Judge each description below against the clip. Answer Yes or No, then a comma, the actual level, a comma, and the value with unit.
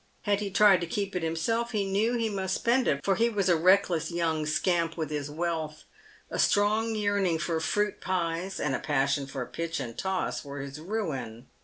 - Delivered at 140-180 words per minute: No, average, 200 wpm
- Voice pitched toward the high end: No, medium, 175 Hz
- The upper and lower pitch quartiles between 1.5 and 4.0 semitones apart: No, average, 4.7 semitones